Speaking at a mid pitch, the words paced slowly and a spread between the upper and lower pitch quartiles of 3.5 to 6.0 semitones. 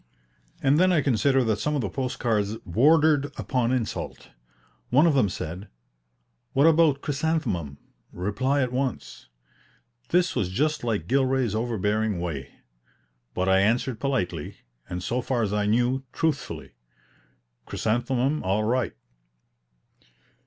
No: low, 120 Hz; slow, 130 wpm; average, 5.1 semitones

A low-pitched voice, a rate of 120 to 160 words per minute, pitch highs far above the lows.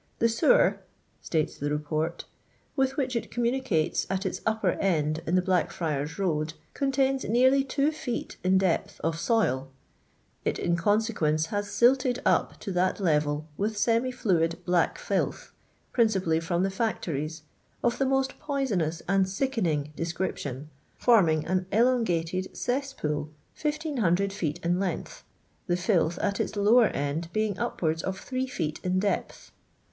No: high, 190 Hz; average, 145 wpm; wide, 6.5 semitones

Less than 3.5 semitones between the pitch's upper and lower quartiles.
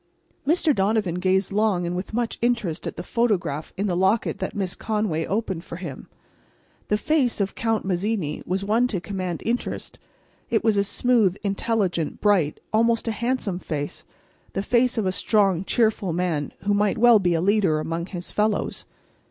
No: average, 3.9 semitones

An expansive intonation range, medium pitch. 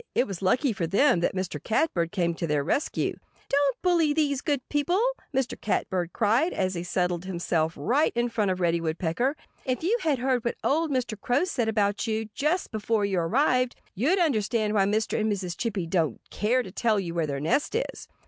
No: wide, 7.0 semitones; high, 215 Hz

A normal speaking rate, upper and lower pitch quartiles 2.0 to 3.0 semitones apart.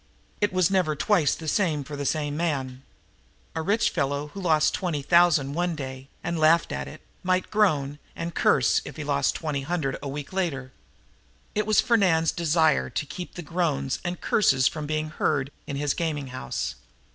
No: average, 180 wpm; average, 3.8 semitones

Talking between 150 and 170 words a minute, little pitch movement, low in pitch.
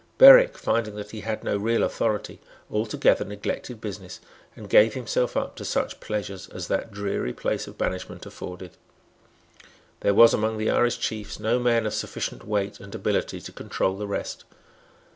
Yes: average, 165 wpm; narrow, 2.1 semitones; low, 105 Hz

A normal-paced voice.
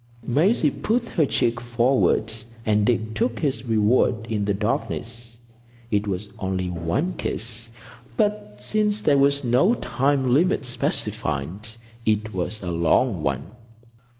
No: slow, 130 wpm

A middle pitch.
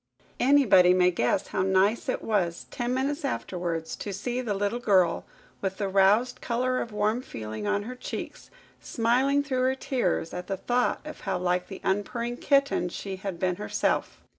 No: high, 205 Hz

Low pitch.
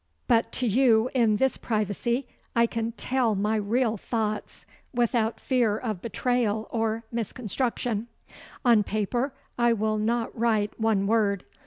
No: high, 225 Hz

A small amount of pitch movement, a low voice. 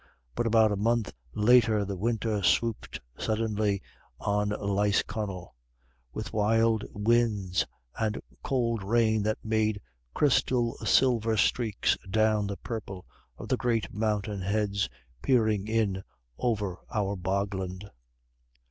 Yes: narrow, 2.1 semitones; low, 105 Hz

